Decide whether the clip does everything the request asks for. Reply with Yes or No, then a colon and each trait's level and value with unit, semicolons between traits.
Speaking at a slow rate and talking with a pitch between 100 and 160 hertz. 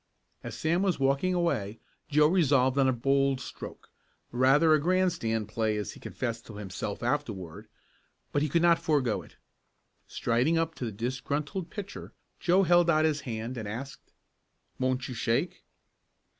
No: average, 155 wpm; low, 135 Hz